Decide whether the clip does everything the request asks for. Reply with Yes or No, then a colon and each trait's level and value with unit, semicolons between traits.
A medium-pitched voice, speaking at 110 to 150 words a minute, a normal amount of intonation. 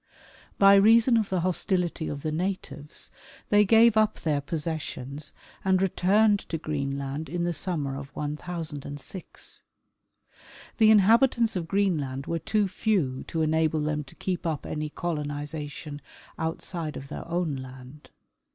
Yes: medium, 160 Hz; average, 140 wpm; average, 4.6 semitones